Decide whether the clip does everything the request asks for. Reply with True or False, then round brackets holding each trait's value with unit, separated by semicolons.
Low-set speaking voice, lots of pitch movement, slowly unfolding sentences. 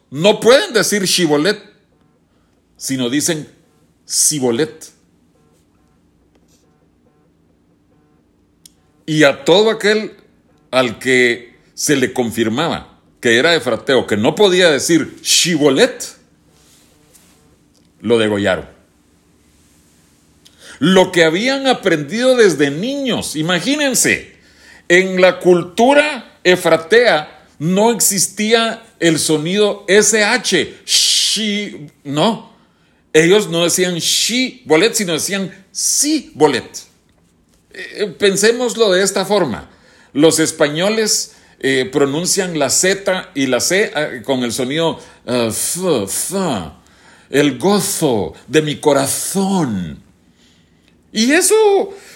False (165 Hz; 8.8 semitones; 95 wpm)